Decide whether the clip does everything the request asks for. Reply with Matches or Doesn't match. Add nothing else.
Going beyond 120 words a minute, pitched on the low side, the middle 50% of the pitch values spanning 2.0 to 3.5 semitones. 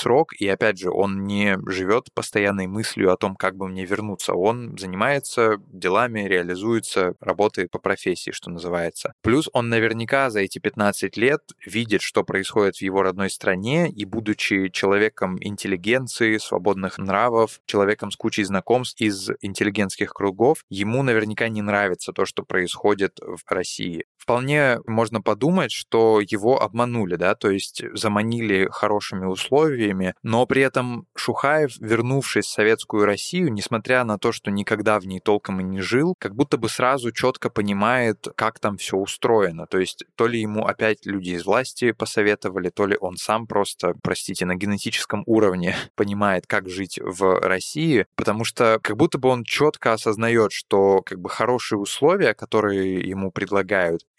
Matches